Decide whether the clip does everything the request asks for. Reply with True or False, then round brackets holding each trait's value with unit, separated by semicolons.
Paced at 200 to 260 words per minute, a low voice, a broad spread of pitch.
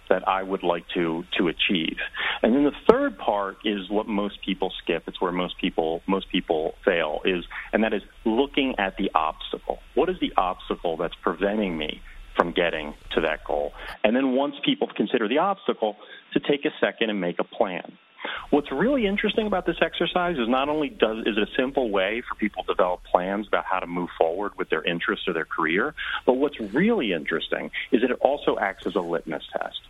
True (205 wpm; 105 Hz; 8.7 semitones)